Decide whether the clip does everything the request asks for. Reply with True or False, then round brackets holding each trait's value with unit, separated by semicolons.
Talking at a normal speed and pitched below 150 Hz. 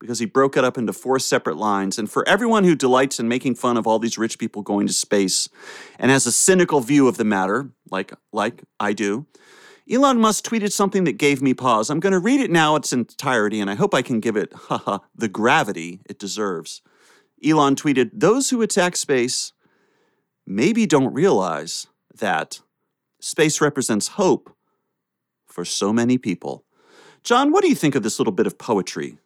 True (190 wpm; 135 Hz)